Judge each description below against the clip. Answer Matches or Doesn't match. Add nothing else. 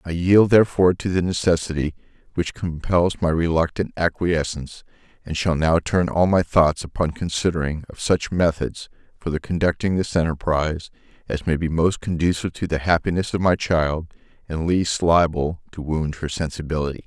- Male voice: Matches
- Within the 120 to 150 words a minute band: Doesn't match